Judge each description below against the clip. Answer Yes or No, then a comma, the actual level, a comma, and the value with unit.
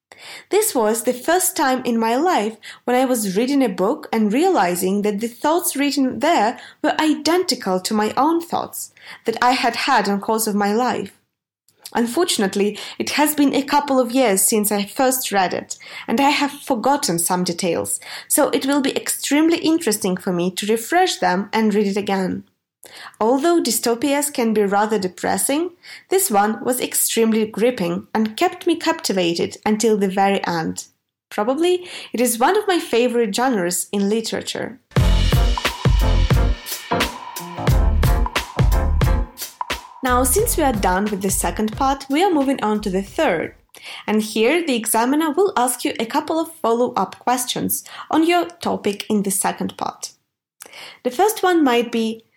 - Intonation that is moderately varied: No, wide, 5.8 semitones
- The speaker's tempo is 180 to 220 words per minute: No, average, 160 wpm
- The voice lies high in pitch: Yes, high, 235 Hz